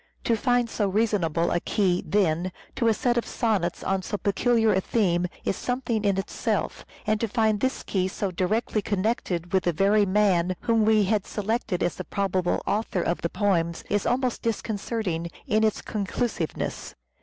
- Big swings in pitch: No, average, 3.4 semitones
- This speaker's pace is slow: No, average, 180 wpm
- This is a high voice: Yes, high, 205 Hz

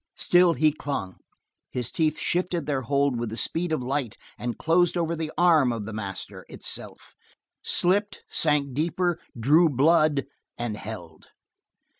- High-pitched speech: No, medium, 145 Hz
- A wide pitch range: Yes, wide, 5.7 semitones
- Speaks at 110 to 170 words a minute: Yes, average, 145 wpm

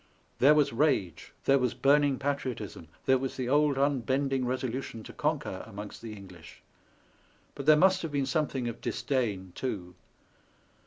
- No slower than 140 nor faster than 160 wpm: Yes, average, 155 wpm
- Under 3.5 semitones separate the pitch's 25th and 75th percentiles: No, average, 4.1 semitones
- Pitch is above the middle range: No, low, 130 Hz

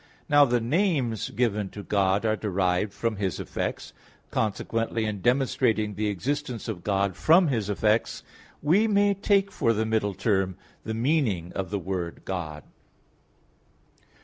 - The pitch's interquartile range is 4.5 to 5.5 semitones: Yes, average, 4.8 semitones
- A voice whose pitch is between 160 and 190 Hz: No, low, 110 Hz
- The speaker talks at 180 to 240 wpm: No, average, 145 wpm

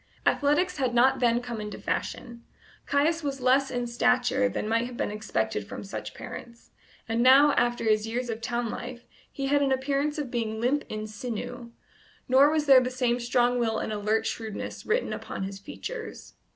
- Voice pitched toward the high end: Yes, high, 245 Hz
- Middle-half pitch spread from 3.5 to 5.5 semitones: No, average, 3.1 semitones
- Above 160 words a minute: Yes, average, 185 wpm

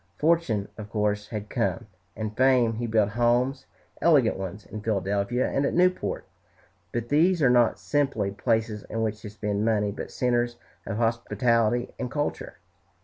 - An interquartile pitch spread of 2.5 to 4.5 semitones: Yes, average, 3.0 semitones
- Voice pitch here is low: Yes, low, 115 Hz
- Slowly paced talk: No, average, 155 wpm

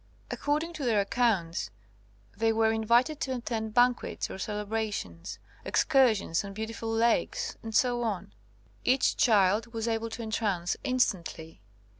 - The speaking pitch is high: Yes, high, 225 Hz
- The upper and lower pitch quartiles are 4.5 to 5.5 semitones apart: No, average, 2.8 semitones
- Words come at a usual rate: No, slow, 120 wpm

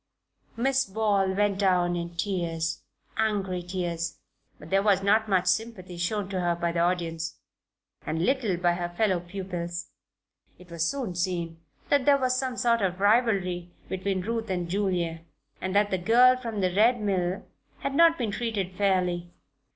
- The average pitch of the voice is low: No, high, 190 Hz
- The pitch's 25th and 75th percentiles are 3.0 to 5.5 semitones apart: Yes, average, 3.8 semitones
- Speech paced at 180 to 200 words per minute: No, average, 165 wpm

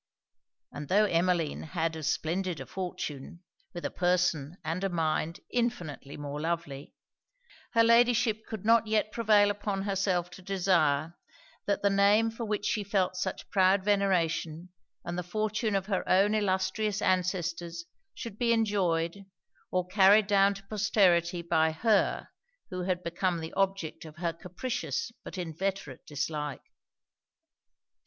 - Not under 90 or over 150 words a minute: Yes, average, 140 wpm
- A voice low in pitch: No, medium, 185 Hz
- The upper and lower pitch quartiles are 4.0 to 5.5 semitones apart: No, average, 3.4 semitones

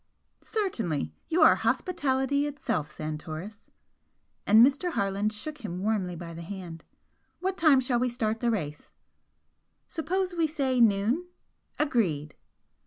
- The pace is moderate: No, slow, 125 wpm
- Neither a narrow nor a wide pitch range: No, wide, 8.3 semitones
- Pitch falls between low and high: No, high, 230 Hz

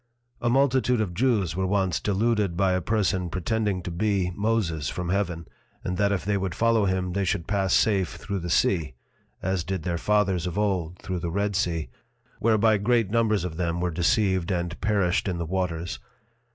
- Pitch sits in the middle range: No, very low, 95 Hz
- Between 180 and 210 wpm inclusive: Yes, average, 190 wpm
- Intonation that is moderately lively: Yes, average, 3.2 semitones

